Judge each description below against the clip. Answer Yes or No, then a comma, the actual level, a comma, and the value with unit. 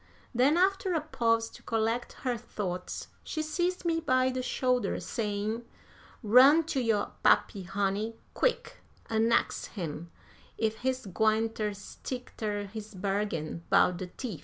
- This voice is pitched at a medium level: No, high, 225 Hz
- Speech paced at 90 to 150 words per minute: Yes, average, 145 wpm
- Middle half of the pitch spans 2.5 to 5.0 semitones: Yes, average, 4.0 semitones